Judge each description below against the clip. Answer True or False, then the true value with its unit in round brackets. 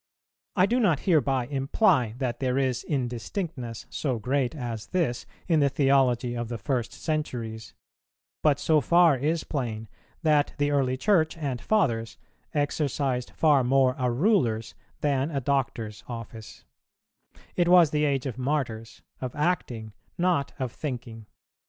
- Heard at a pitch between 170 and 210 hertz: False (135 Hz)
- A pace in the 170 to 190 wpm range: False (140 wpm)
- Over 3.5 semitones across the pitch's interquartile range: True (4.1 semitones)